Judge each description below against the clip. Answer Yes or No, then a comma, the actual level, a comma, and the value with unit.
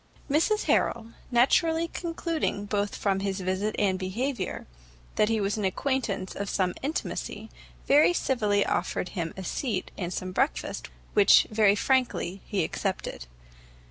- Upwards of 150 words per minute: No, average, 140 wpm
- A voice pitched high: Yes, high, 205 Hz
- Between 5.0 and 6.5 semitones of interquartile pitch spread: Yes, wide, 5.6 semitones